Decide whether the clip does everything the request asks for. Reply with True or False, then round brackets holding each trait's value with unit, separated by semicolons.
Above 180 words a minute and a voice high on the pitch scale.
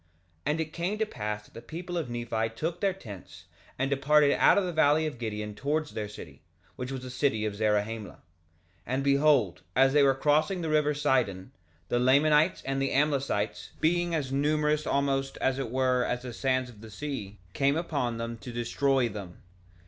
False (195 wpm; 135 Hz)